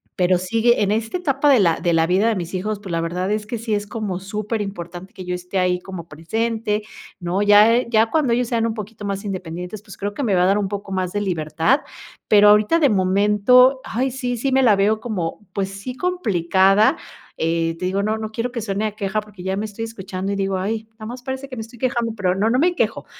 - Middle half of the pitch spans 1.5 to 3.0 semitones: No, average, 3.4 semitones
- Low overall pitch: No, high, 205 Hz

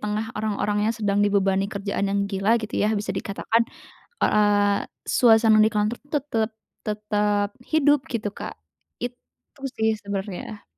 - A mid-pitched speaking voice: No, high, 210 Hz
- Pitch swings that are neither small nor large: No, narrow, 1.7 semitones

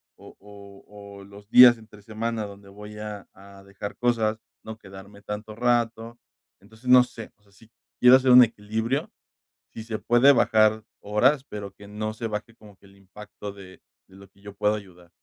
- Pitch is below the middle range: Yes, low, 105 Hz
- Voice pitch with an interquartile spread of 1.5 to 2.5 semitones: Yes, narrow, 2.2 semitones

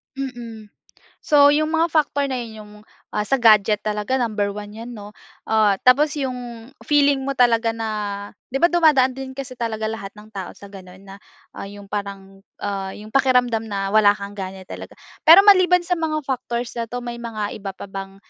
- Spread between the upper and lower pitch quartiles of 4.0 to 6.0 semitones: Yes, average, 4.7 semitones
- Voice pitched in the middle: No, high, 230 Hz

